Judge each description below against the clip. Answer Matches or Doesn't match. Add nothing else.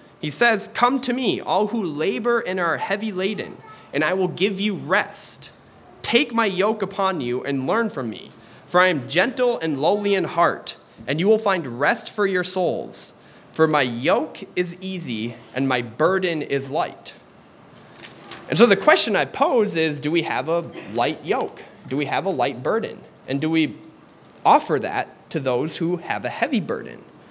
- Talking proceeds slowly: Doesn't match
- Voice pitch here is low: Doesn't match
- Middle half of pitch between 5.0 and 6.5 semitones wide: Matches